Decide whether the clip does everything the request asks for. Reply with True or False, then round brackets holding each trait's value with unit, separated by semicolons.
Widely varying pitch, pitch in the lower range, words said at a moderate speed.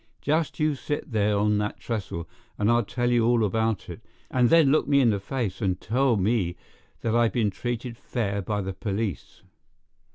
False (3.2 semitones; 115 Hz; 190 wpm)